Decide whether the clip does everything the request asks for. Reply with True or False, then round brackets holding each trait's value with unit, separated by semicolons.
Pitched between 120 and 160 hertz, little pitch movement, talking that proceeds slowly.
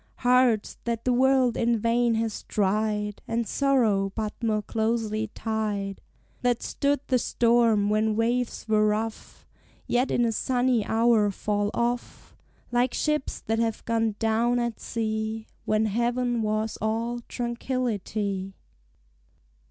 False (225 Hz; 2.1 semitones; 130 wpm)